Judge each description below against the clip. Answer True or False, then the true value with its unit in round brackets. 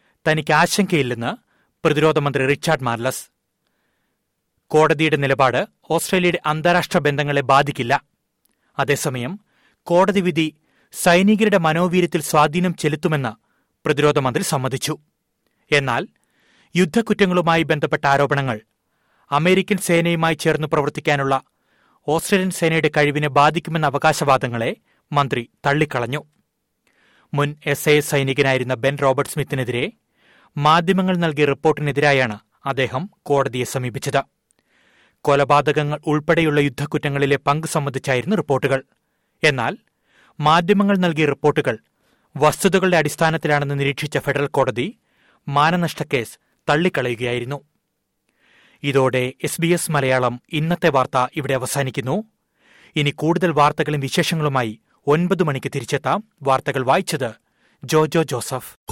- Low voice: False (150 Hz)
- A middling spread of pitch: True (3.0 semitones)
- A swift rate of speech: False (90 wpm)